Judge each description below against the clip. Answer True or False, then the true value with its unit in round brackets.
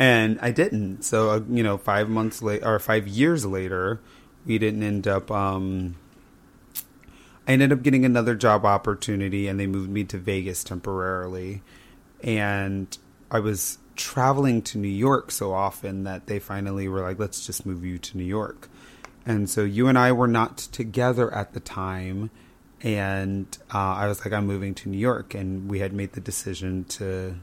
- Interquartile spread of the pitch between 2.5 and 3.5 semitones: True (3.0 semitones)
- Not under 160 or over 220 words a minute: True (175 wpm)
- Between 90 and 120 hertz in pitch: True (100 Hz)